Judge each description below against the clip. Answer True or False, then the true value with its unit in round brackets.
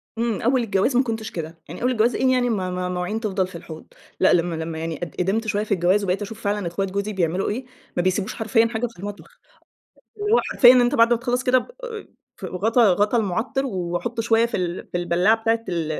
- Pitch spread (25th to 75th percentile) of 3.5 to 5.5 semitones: True (4.5 semitones)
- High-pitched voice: True (210 Hz)